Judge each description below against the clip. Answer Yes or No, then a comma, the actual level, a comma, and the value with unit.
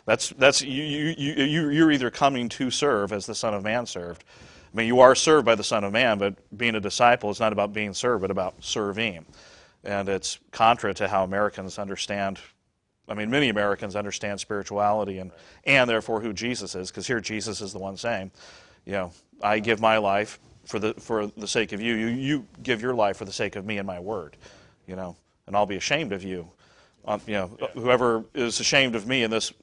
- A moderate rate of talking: No, fast, 215 wpm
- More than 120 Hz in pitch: No, low, 105 Hz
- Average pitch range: Yes, average, 3.3 semitones